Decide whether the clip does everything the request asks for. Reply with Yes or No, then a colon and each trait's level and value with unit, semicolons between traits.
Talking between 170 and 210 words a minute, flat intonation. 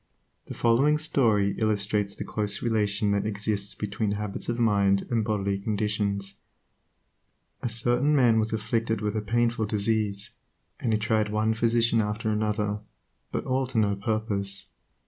No: average, 145 wpm; narrow, 1.9 semitones